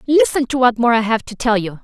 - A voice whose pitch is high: Yes, high, 240 Hz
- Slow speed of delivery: No, fast, 295 wpm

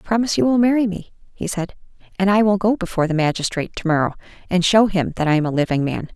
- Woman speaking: Yes, female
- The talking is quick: Yes, fast, 245 wpm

